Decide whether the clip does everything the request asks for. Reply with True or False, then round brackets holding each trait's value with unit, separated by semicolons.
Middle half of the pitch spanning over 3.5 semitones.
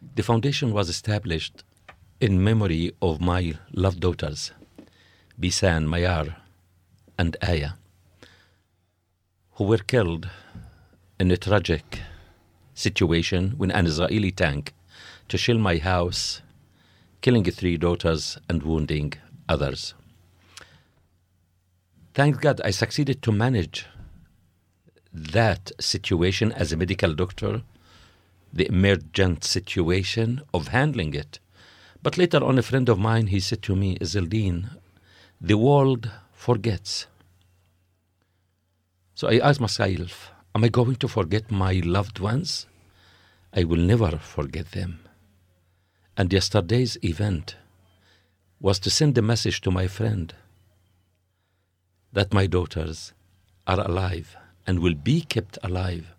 False (3.0 semitones)